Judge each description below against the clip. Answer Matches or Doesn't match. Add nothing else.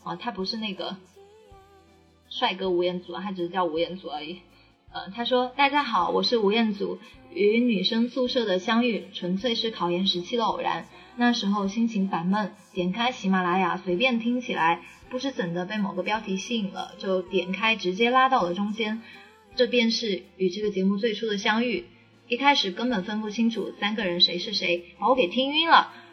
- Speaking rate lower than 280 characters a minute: Doesn't match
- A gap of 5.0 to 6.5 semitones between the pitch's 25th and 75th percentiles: Doesn't match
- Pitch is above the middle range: Matches